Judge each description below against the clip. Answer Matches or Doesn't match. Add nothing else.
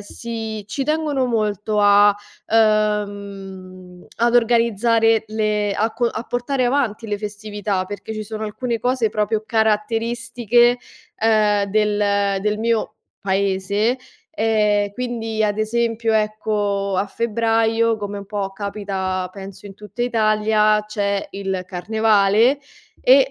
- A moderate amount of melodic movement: Doesn't match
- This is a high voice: Matches